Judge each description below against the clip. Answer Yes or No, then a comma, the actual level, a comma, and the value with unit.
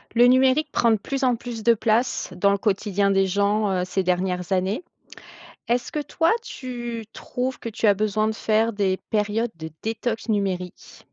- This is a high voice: Yes, high, 215 Hz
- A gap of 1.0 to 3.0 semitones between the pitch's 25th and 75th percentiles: No, average, 3.4 semitones